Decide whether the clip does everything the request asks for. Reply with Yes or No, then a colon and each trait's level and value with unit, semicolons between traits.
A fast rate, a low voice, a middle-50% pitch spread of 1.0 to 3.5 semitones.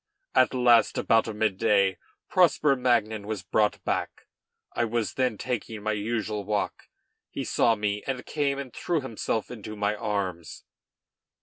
No: average, 145 wpm; low, 110 Hz; average, 3.0 semitones